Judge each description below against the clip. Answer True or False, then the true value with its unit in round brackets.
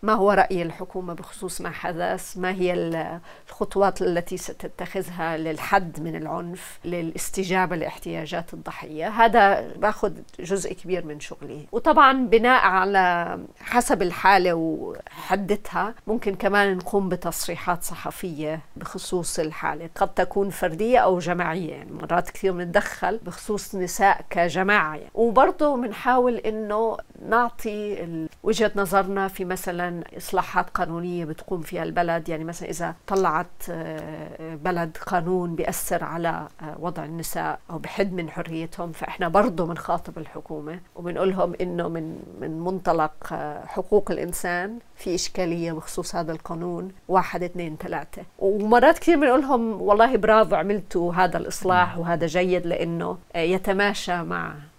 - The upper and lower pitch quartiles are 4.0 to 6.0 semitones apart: False (2.8 semitones)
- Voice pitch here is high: False (180 Hz)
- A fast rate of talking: False (120 wpm)